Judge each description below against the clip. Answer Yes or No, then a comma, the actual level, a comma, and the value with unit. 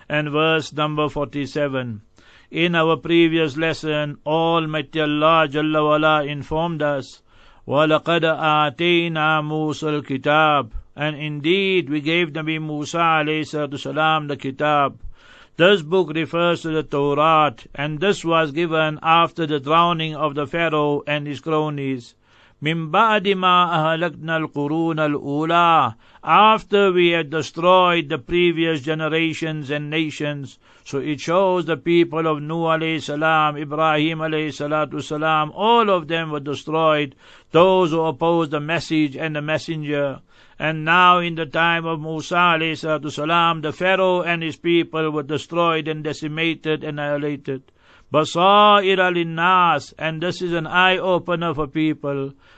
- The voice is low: No, medium, 155 Hz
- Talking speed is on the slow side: Yes, slow, 130 wpm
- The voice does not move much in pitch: Yes, narrow, 1.9 semitones